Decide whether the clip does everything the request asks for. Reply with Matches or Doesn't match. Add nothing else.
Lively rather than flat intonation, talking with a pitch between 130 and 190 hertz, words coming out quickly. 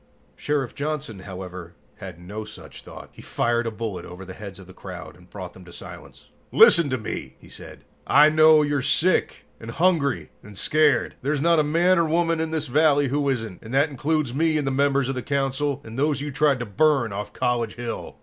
Matches